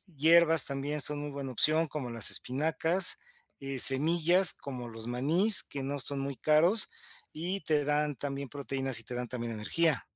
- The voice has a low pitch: No, medium, 145 Hz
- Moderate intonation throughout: Yes, average, 3.4 semitones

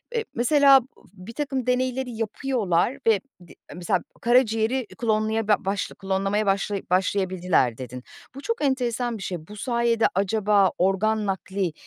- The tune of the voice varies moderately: Yes, average, 4.3 semitones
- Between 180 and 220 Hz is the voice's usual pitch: Yes, high, 215 Hz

